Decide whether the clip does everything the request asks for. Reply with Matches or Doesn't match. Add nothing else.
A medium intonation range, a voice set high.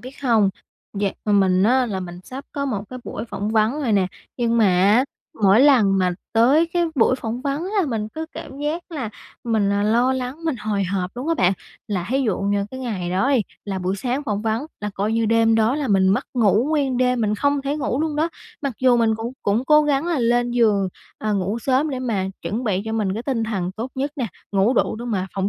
Matches